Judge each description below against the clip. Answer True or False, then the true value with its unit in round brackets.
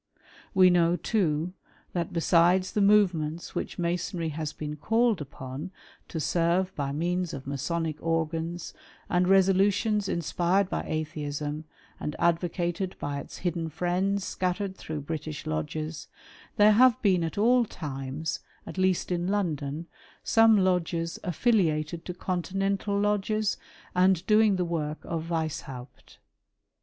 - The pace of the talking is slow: True (125 wpm)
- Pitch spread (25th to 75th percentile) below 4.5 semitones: True (3.5 semitones)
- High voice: False (175 Hz)